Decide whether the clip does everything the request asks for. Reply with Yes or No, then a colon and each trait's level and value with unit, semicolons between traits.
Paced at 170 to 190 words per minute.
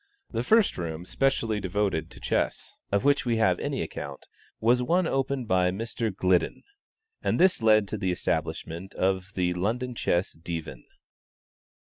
No: average, 150 wpm